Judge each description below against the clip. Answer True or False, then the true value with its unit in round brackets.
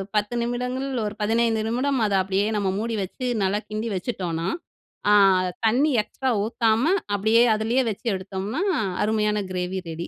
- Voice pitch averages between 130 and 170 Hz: False (220 Hz)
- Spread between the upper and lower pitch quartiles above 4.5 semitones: False (3.5 semitones)